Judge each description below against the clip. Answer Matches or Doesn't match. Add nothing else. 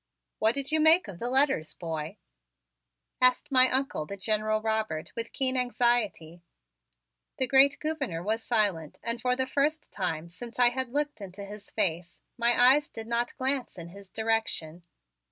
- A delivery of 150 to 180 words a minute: Matches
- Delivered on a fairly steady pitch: Doesn't match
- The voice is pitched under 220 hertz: Doesn't match